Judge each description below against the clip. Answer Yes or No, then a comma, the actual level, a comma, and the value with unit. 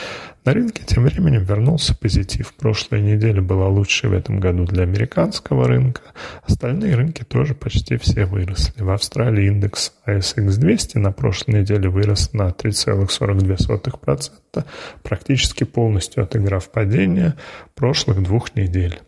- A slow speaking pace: No, average, 125 wpm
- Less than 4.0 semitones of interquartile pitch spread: No, average, 4.3 semitones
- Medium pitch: No, low, 105 Hz